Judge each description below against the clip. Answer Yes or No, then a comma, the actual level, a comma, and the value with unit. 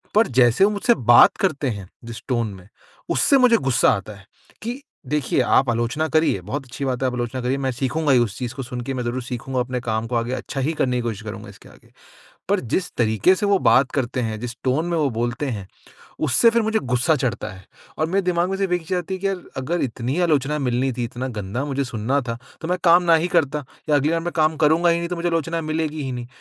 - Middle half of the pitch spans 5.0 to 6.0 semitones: Yes, wide, 5.5 semitones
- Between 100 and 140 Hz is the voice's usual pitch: Yes, low, 135 Hz